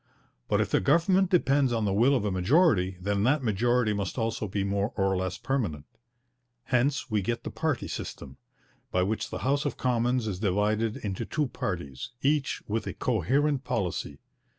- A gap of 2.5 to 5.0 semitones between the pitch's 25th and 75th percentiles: No, wide, 5.5 semitones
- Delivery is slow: No, average, 175 wpm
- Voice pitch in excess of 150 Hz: No, low, 115 Hz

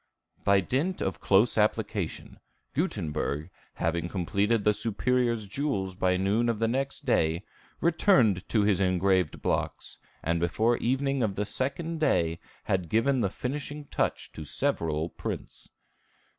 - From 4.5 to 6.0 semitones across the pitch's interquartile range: Yes, wide, 5.6 semitones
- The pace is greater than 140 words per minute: No, slow, 135 wpm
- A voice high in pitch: No, low, 105 Hz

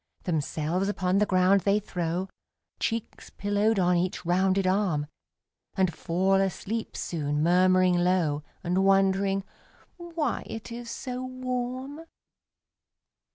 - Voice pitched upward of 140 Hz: Yes, high, 190 Hz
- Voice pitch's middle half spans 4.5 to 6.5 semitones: No, average, 3.3 semitones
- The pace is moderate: No, slow, 110 wpm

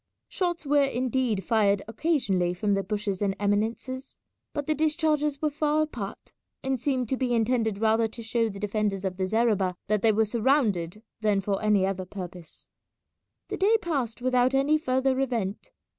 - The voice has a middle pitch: No, high, 225 Hz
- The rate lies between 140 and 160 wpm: No, average, 170 wpm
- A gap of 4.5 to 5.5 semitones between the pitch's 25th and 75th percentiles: Yes, average, 5.0 semitones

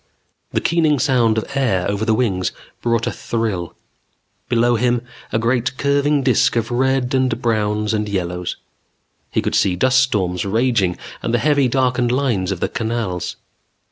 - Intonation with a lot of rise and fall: No, average, 3.8 semitones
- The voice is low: Yes, low, 115 Hz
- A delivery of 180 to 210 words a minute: No, average, 160 wpm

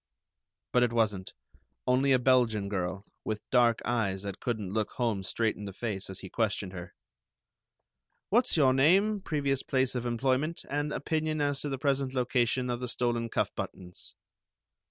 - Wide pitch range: No, average, 4.6 semitones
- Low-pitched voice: Yes, low, 120 Hz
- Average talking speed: Yes, average, 165 wpm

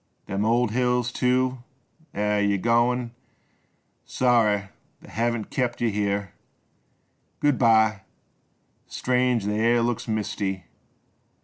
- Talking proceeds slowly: Yes, slow, 110 wpm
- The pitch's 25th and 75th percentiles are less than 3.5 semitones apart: Yes, average, 2.9 semitones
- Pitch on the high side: No, low, 115 Hz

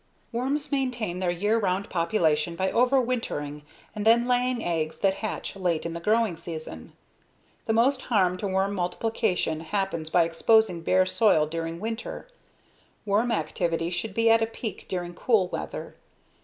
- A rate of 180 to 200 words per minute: No, average, 155 wpm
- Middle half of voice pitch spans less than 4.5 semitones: No, average, 5.1 semitones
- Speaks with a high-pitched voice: Yes, high, 195 Hz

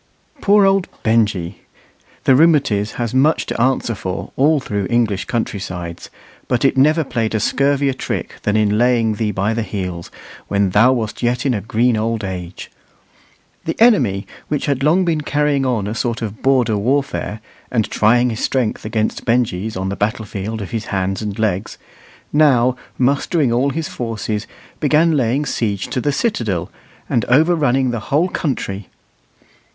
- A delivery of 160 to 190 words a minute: Yes, average, 165 wpm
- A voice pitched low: Yes, low, 115 Hz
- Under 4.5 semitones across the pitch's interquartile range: No, average, 4.8 semitones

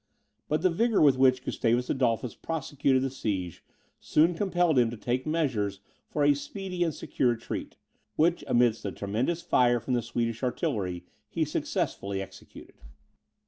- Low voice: Yes, low, 130 Hz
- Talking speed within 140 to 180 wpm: Yes, average, 150 wpm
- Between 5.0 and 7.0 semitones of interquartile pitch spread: Yes, average, 5.3 semitones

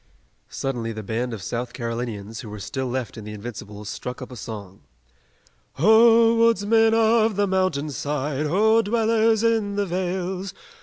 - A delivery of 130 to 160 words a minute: Yes, average, 155 wpm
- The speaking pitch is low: No, medium, 150 Hz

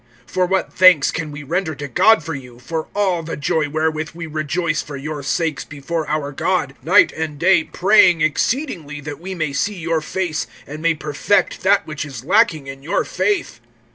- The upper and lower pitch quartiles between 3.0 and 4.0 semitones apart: Yes, average, 3.7 semitones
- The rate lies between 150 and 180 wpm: No, average, 190 wpm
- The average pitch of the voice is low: No, medium, 160 Hz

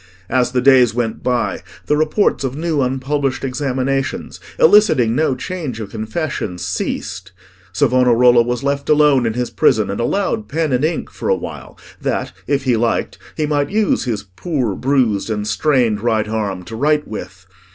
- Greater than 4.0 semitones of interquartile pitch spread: Yes, average, 4.6 semitones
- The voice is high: No, low, 125 Hz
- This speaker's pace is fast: No, average, 165 wpm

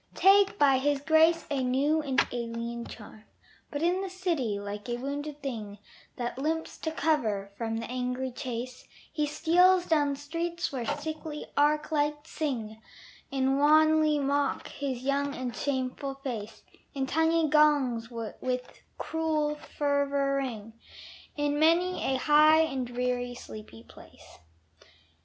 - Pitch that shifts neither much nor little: Yes, average, 3.9 semitones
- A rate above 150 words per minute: No, slow, 135 wpm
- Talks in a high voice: Yes, very high, 280 Hz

